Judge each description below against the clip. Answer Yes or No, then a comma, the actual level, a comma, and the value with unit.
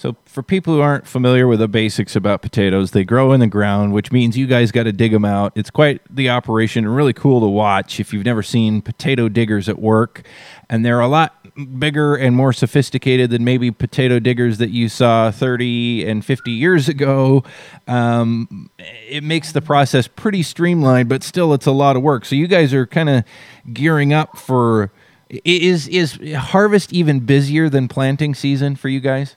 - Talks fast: No, average, 195 wpm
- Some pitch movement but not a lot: Yes, average, 3.8 semitones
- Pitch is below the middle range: Yes, low, 130 Hz